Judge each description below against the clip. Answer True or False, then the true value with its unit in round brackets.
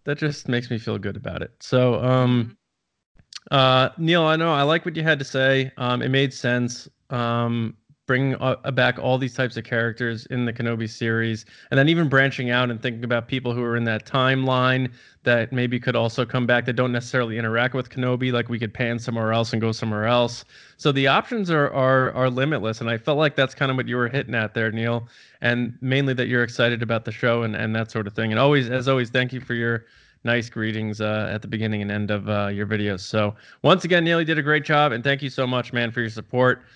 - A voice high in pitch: False (125 Hz)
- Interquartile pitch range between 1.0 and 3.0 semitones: True (2.4 semitones)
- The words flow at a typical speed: False (240 wpm)